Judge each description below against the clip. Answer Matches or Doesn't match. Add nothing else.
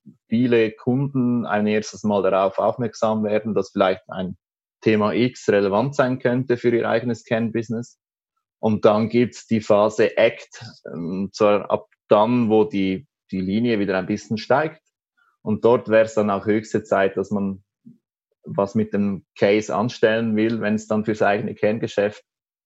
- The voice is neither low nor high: Doesn't match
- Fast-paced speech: Doesn't match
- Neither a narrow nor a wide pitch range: Doesn't match